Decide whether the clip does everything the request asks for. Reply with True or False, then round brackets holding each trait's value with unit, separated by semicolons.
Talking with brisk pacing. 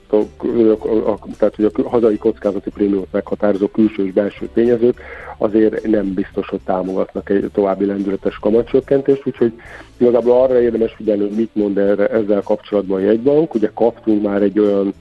True (170 wpm)